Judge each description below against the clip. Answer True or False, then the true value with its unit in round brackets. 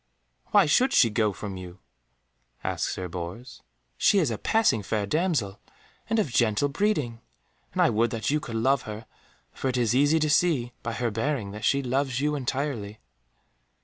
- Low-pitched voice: True (120 Hz)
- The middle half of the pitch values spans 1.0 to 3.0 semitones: False (5.4 semitones)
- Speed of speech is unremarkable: True (180 wpm)